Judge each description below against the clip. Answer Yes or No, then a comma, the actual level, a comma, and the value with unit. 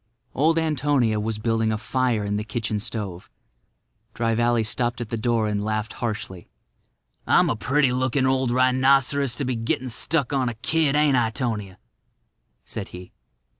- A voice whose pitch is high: No, low, 120 Hz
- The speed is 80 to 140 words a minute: No, average, 165 wpm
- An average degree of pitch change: Yes, average, 3.2 semitones